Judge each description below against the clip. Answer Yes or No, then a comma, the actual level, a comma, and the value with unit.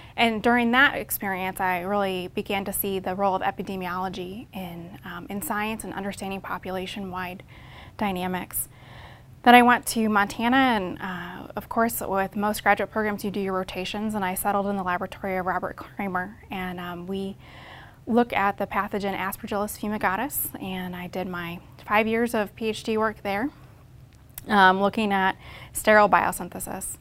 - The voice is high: Yes, high, 195 Hz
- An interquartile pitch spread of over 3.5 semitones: No, narrow, 2.4 semitones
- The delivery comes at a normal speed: Yes, average, 160 wpm